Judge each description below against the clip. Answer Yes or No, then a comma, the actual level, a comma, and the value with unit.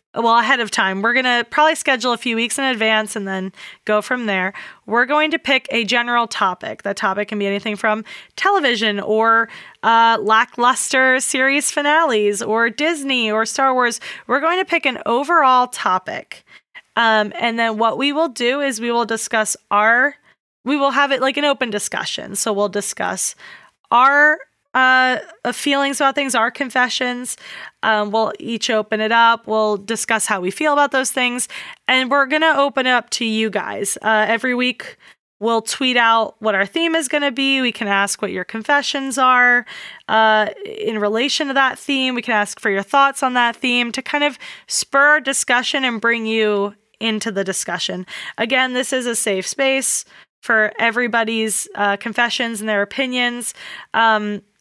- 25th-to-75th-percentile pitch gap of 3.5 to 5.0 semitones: Yes, average, 3.8 semitones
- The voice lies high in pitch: Yes, high, 240 Hz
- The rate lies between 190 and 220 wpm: No, average, 180 wpm